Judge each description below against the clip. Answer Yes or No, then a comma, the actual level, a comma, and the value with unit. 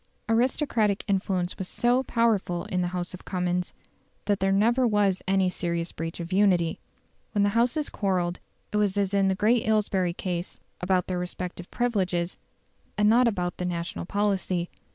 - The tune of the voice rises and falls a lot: No, average, 2.8 semitones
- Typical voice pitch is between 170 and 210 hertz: Yes, high, 190 Hz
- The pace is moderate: Yes, average, 165 wpm